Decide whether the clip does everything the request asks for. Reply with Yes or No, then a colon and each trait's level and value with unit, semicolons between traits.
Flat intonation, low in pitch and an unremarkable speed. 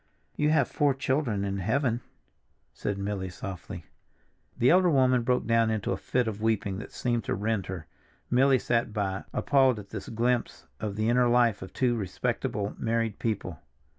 No: average, 3.7 semitones; low, 115 Hz; average, 170 wpm